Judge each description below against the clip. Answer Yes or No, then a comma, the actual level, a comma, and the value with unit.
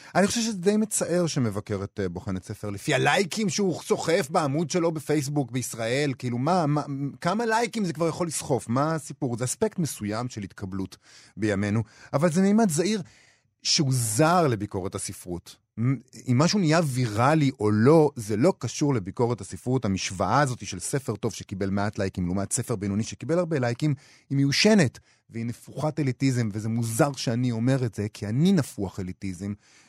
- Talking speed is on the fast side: Yes, fast, 165 wpm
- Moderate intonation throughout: No, wide, 7.1 semitones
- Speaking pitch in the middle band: No, low, 130 Hz